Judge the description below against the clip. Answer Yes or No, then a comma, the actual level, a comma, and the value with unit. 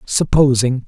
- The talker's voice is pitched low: Yes, low, 130 Hz